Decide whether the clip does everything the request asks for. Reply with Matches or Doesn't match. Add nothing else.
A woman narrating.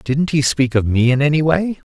Doesn't match